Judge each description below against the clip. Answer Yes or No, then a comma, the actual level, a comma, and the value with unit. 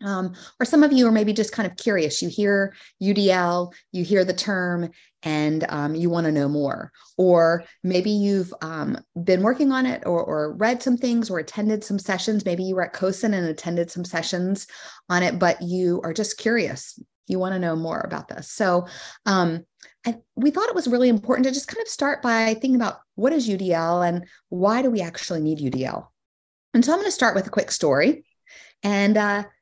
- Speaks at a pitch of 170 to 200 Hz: Yes, high, 190 Hz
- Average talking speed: No, fast, 210 wpm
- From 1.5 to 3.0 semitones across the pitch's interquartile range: No, average, 4.5 semitones